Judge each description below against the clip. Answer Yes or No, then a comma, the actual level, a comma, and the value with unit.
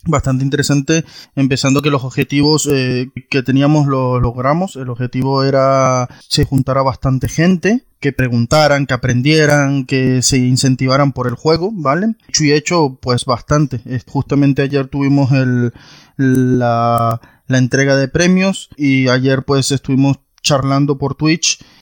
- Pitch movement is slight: Yes, narrow, 1.9 semitones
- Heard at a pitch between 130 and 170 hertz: Yes, low, 135 Hz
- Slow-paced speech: No, average, 140 wpm